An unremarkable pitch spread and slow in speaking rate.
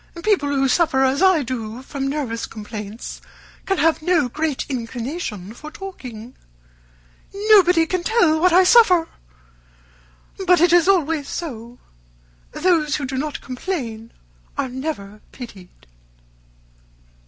No: wide, 6.2 semitones; slow, 120 wpm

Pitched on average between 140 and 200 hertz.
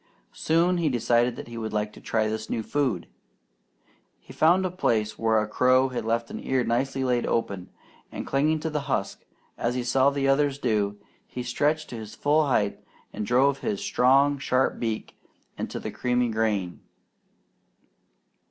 No: low, 125 Hz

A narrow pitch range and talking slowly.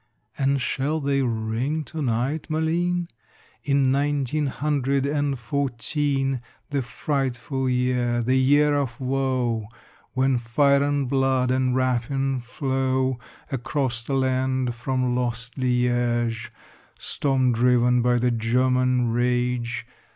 Yes: narrow, 2.1 semitones; slow, 115 wpm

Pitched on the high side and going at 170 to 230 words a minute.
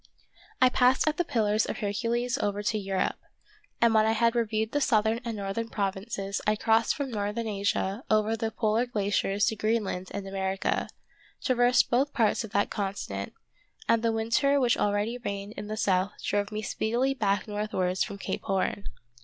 Yes: high, 215 Hz; average, 175 wpm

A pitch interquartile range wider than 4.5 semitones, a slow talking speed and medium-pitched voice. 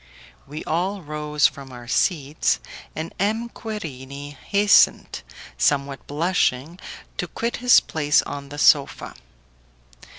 Yes: average, 4.9 semitones; slow, 110 wpm; medium, 150 Hz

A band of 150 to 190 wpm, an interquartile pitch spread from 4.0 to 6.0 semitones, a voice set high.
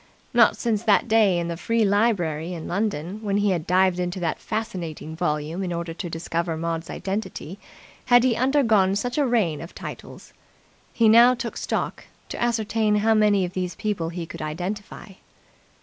Yes: average, 175 wpm; average, 4.6 semitones; high, 195 Hz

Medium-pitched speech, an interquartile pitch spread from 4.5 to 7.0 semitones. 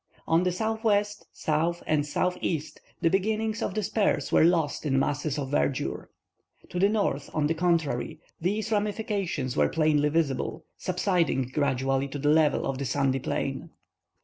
Yes: medium, 160 Hz; wide, 5.5 semitones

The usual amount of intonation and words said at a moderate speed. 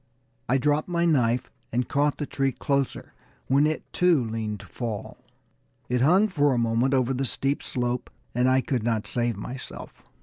Yes: average, 3.2 semitones; average, 175 wpm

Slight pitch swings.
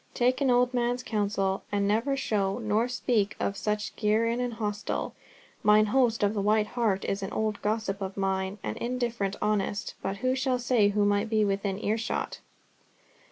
No: average, 3.0 semitones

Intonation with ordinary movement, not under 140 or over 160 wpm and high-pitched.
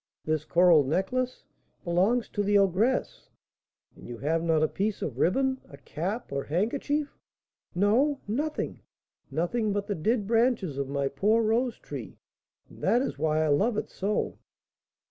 No: wide, 6.9 semitones; average, 155 wpm; high, 200 Hz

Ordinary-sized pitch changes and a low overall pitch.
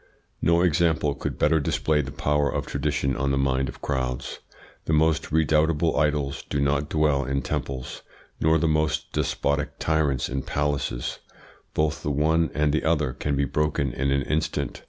No: narrow, 2.1 semitones; very low, 75 Hz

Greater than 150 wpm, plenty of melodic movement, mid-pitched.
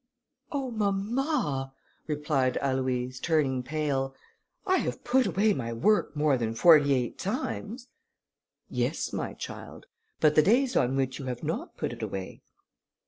No: average, 140 wpm; wide, 8.2 semitones; medium, 145 Hz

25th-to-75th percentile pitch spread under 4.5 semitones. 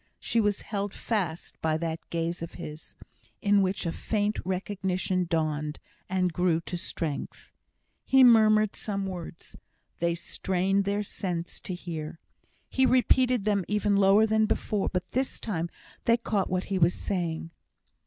Yes: average, 3.6 semitones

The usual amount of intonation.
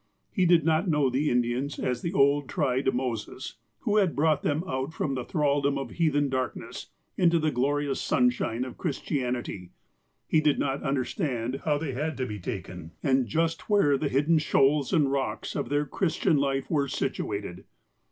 Yes: average, 3.2 semitones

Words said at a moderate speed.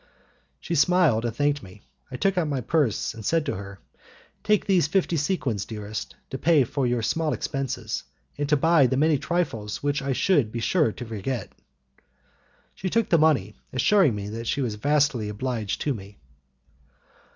Yes: average, 180 wpm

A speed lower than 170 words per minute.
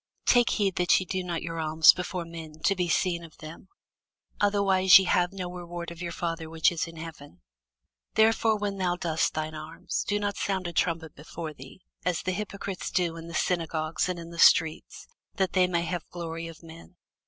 No: average, 200 wpm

